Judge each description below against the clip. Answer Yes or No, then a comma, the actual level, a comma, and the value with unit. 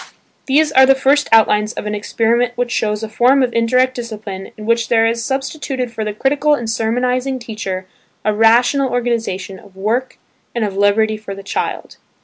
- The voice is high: Yes, high, 230 Hz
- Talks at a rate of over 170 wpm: Yes, average, 180 wpm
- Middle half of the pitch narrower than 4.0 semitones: Yes, average, 3.1 semitones